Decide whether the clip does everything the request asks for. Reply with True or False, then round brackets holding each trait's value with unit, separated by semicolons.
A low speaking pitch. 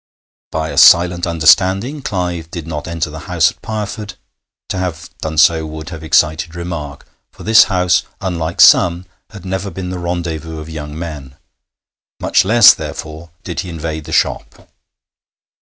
True (85 Hz)